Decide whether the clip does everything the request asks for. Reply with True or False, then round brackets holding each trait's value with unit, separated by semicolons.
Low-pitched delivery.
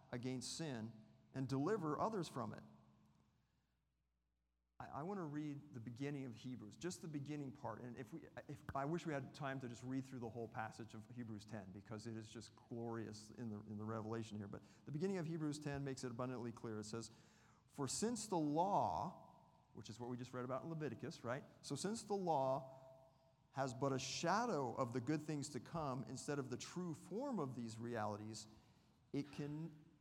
True (130 Hz)